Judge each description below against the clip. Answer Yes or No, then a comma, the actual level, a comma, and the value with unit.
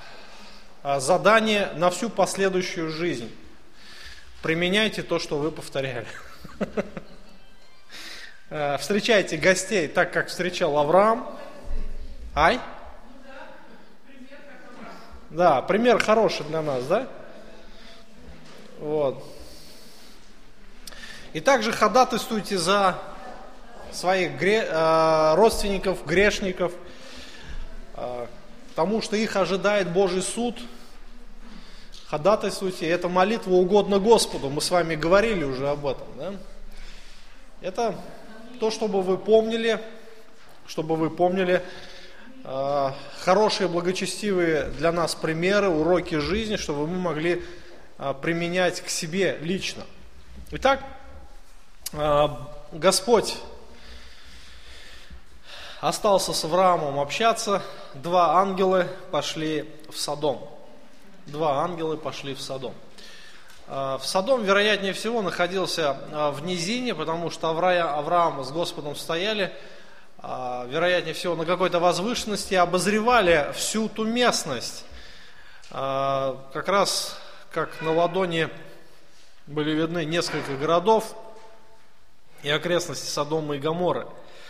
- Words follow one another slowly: Yes, slow, 90 wpm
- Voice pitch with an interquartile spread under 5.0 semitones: Yes, average, 4.6 semitones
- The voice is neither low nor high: Yes, medium, 180 Hz